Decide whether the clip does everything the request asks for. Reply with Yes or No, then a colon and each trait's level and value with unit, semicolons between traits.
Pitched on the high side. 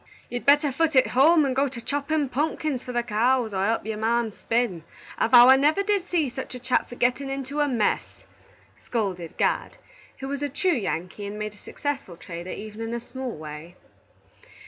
Yes: high, 245 Hz